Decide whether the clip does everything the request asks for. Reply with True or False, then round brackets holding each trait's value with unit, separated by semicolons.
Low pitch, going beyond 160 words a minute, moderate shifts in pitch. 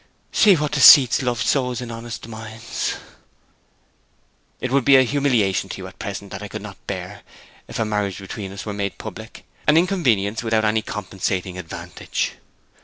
True (110 Hz; 170 wpm; 4.2 semitones)